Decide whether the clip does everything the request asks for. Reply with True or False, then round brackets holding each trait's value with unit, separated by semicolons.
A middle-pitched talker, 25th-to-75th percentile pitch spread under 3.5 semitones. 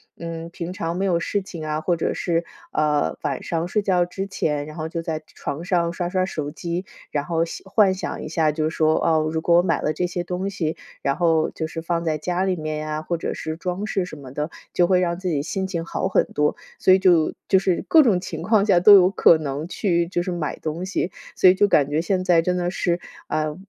True (170 Hz; 2.8 semitones)